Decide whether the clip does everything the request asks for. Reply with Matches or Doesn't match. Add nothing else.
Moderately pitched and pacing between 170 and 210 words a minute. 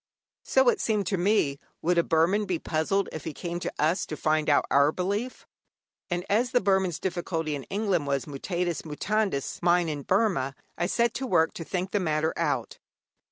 Matches